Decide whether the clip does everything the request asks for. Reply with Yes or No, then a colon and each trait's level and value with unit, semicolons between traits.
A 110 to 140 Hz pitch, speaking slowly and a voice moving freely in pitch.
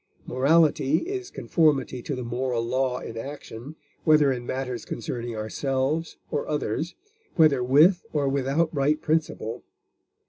No: low, 135 Hz; slow, 130 wpm; average, 3.7 semitones